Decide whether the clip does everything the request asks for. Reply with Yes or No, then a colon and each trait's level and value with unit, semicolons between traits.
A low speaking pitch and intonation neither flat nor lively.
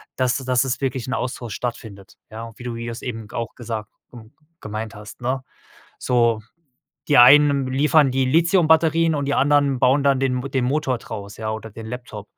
Yes: low, 125 Hz; average, 3.4 semitones